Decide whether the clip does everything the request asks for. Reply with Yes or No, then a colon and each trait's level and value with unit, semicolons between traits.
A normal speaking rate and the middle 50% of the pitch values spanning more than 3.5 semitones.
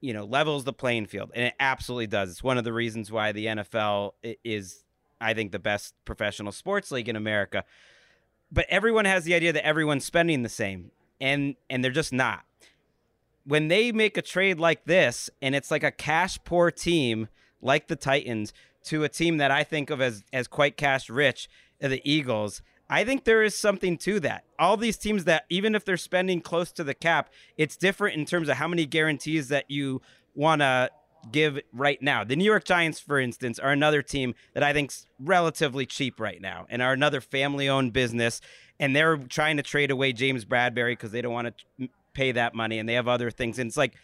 No: fast, 210 wpm; average, 5.0 semitones